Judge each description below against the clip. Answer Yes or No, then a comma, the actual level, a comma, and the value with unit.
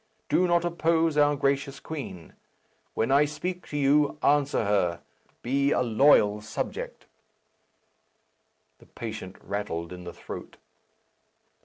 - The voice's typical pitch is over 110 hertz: Yes, medium, 140 Hz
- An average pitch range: No, wide, 6.1 semitones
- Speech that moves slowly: Yes, slow, 120 wpm